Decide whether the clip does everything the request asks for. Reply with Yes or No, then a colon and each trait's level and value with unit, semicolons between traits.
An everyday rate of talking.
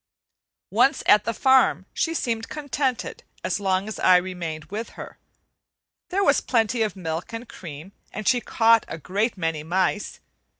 Yes: average, 160 wpm